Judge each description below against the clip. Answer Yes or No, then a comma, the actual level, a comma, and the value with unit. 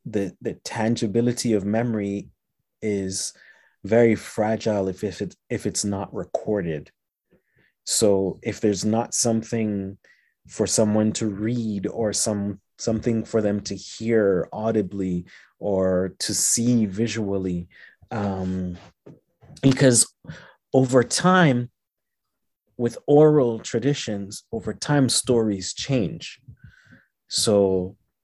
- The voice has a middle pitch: No, low, 110 Hz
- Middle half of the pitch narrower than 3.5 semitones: Yes, average, 2.9 semitones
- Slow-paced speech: Yes, slow, 100 wpm